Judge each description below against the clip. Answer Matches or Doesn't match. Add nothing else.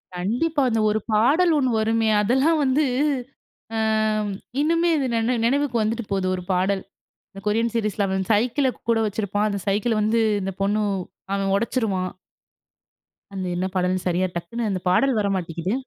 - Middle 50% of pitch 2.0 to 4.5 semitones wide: Matches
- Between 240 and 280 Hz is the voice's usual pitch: Doesn't match